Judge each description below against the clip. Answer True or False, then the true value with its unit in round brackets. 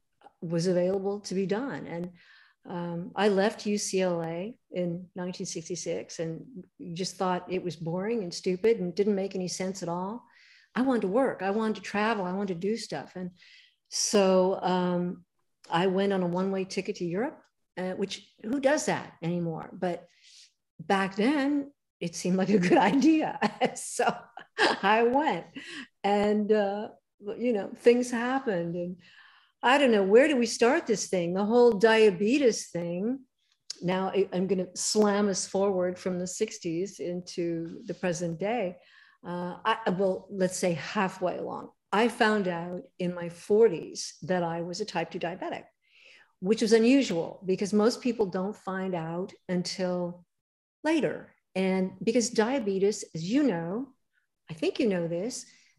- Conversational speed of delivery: True (155 wpm)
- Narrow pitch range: False (3.7 semitones)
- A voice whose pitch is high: True (195 Hz)